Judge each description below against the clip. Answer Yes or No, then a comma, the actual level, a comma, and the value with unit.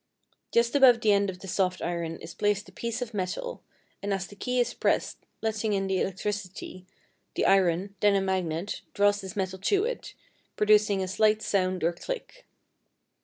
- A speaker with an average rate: Yes, average, 180 wpm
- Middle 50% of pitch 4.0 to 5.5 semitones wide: No, narrow, 2.6 semitones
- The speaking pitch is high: Yes, high, 200 Hz